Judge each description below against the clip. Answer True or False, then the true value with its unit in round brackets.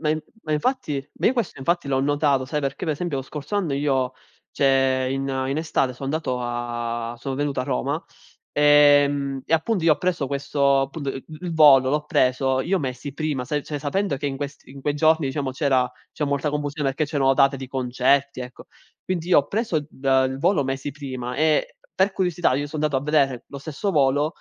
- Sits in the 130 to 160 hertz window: True (140 Hz)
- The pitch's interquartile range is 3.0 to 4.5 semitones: False (2.5 semitones)